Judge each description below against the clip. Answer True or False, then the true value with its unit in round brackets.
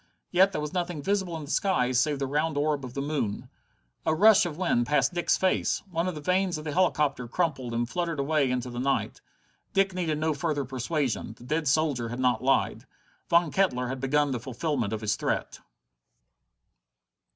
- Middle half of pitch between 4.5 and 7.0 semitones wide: True (4.8 semitones)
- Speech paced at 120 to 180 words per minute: False (195 wpm)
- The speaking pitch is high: False (150 Hz)